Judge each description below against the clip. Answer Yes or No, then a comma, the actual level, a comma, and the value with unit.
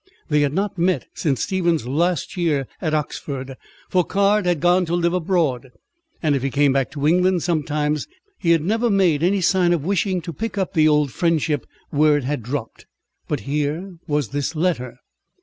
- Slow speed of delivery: No, average, 185 wpm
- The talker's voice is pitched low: No, medium, 160 Hz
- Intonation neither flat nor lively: Yes, average, 3.8 semitones